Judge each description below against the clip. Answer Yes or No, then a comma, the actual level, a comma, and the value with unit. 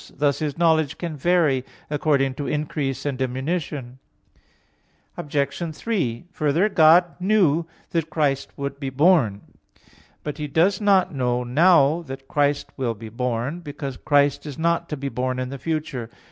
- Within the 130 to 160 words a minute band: Yes, average, 150 wpm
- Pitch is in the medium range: Yes, medium, 145 Hz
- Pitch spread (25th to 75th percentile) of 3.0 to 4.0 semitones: Yes, average, 3.6 semitones